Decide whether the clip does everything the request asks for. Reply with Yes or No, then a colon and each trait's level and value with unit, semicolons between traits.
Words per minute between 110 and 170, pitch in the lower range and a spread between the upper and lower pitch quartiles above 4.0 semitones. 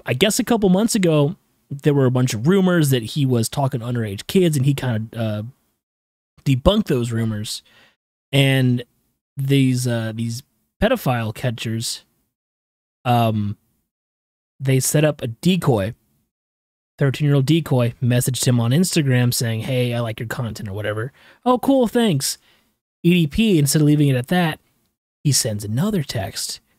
Yes: average, 150 wpm; low, 125 Hz; average, 4.8 semitones